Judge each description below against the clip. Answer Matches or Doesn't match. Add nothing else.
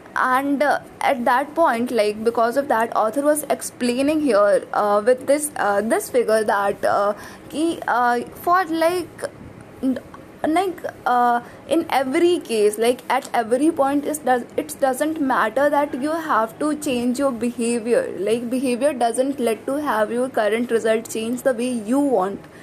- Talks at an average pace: Matches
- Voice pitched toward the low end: Doesn't match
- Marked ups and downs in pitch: Doesn't match